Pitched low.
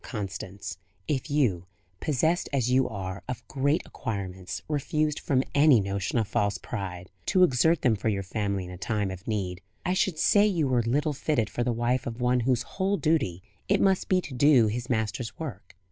Yes: low, 120 Hz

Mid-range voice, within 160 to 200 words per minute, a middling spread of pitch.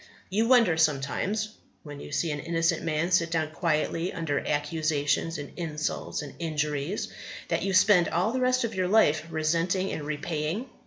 Yes: medium, 165 Hz; average, 165 wpm; average, 3.4 semitones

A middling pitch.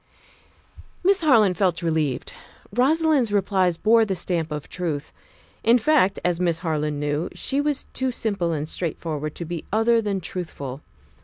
Yes: medium, 180 Hz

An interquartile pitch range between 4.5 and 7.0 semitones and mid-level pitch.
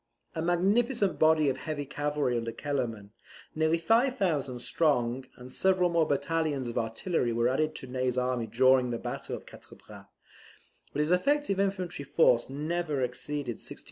Yes: average, 5.2 semitones; medium, 145 Hz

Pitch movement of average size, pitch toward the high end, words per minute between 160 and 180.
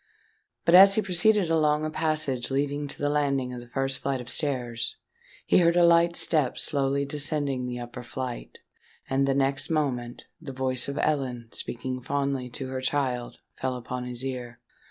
No: average, 3.0 semitones; low, 135 Hz; average, 175 wpm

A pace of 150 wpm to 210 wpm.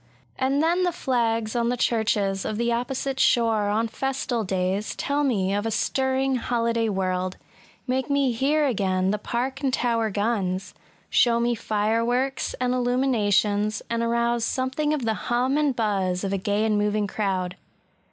Yes: average, 170 wpm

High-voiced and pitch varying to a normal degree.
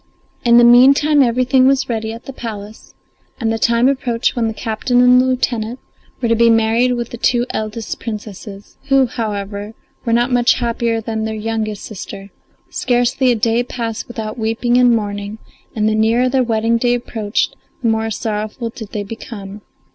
No: high, 230 Hz; narrow, 2.0 semitones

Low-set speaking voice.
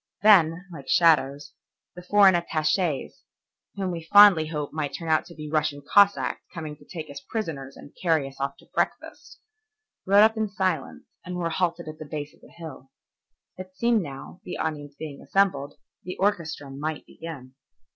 No: medium, 160 Hz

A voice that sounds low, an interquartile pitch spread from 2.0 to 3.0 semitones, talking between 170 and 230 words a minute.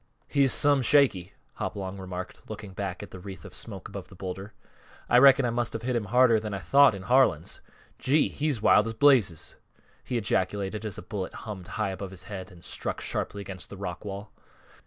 No: low, 105 Hz; average, 4.4 semitones; average, 200 wpm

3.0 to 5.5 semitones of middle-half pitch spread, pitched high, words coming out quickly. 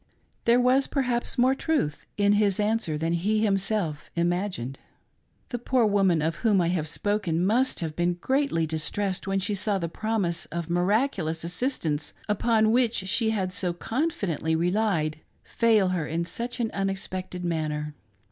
No: average, 4.7 semitones; high, 195 Hz; average, 155 wpm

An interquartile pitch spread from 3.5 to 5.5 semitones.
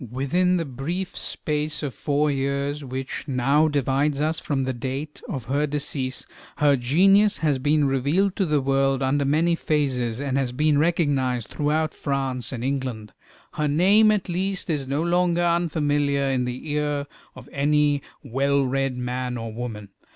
No: average, 2.7 semitones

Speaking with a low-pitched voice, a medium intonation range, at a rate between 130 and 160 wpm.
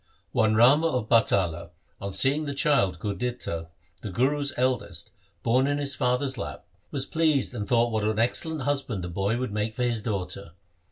No: low, 120 Hz; average, 5.0 semitones; average, 175 wpm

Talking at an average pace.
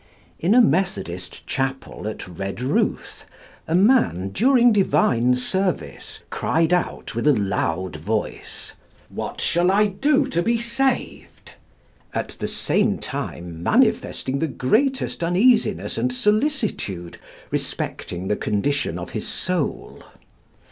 No: slow, 115 wpm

